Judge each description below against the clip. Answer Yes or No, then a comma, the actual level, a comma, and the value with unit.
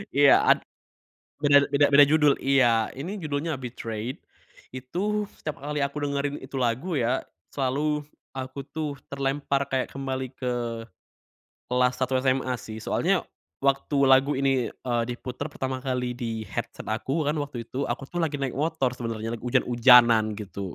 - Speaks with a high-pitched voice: No, low, 135 Hz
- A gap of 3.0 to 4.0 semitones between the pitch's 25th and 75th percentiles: No, narrow, 2.6 semitones